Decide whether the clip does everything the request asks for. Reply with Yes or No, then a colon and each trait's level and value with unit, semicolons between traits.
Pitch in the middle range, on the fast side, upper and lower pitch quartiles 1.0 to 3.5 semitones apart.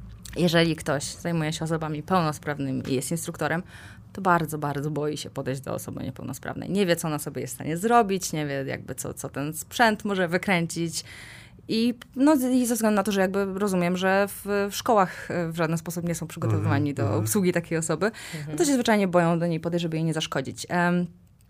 No: medium, 170 Hz; fast, 205 wpm; average, 4.2 semitones